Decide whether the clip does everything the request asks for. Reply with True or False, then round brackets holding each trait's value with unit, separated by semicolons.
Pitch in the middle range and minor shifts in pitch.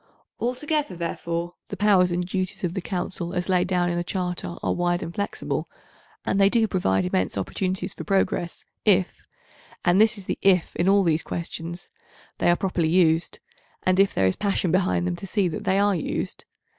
True (180 Hz; 2.3 semitones)